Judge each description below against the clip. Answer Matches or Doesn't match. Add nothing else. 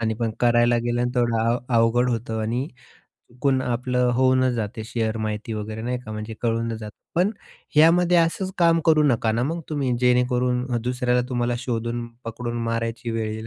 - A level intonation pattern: Matches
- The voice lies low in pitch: Matches